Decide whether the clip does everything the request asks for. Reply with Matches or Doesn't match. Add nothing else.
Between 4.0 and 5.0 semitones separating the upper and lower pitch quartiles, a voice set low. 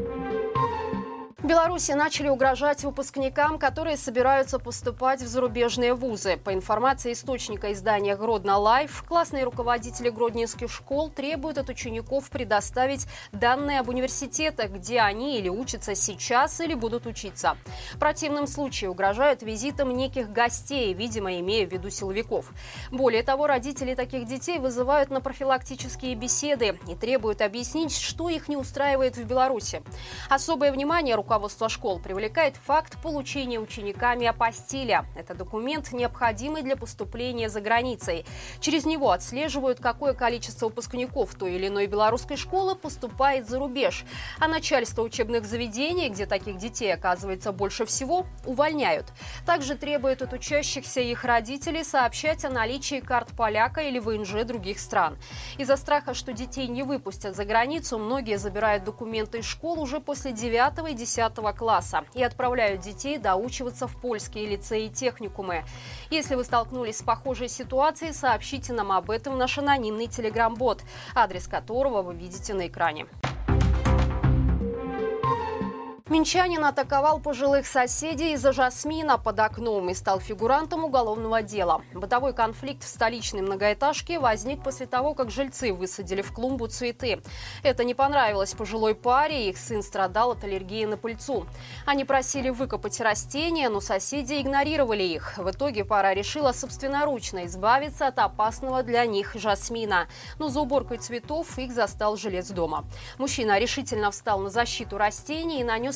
Doesn't match